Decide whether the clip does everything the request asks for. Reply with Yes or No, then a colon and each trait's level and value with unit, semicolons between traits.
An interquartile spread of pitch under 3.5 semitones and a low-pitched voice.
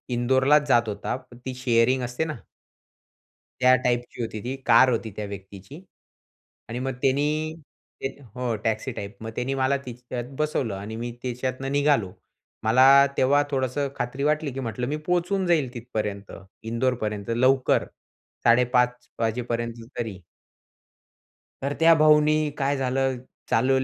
Yes: average, 2.8 semitones; low, 125 Hz